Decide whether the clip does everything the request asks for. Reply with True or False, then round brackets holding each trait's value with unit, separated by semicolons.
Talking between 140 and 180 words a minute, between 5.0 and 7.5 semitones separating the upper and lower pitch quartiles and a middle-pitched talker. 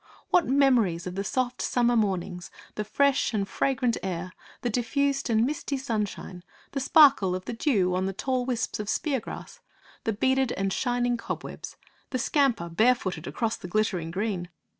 False (160 wpm; 5.5 semitones; 230 Hz)